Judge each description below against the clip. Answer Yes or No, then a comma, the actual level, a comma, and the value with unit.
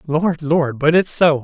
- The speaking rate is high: Yes, fast, 210 wpm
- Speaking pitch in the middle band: Yes, medium, 155 Hz